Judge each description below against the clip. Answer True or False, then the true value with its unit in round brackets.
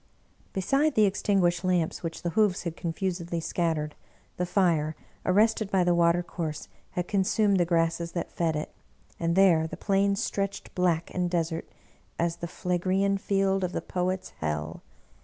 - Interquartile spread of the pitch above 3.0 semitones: False (2.6 semitones)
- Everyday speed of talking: True (165 wpm)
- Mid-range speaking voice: True (175 Hz)